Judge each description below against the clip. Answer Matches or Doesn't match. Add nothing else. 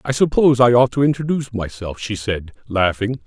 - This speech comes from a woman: Doesn't match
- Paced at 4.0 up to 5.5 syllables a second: Doesn't match